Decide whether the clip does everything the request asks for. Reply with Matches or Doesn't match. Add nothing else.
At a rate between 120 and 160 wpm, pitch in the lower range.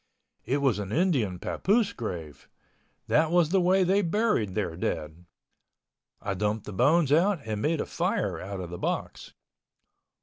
Matches